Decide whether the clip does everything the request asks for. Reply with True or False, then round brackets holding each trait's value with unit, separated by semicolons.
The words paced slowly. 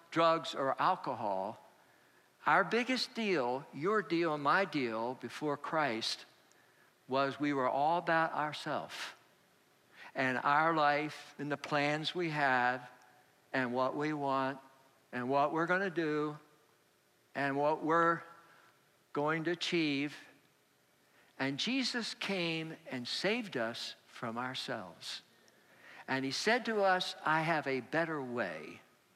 True (125 wpm)